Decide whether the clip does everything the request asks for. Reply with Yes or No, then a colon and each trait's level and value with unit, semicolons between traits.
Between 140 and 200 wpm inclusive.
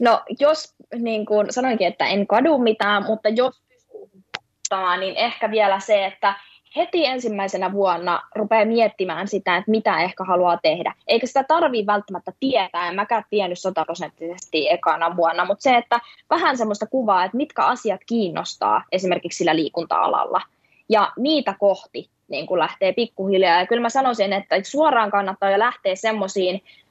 Yes: average, 150 wpm